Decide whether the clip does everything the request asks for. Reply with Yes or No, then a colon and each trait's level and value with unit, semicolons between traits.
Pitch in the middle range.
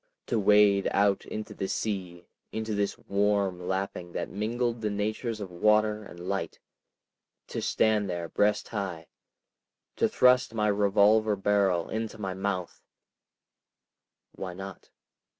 No: low, 100 Hz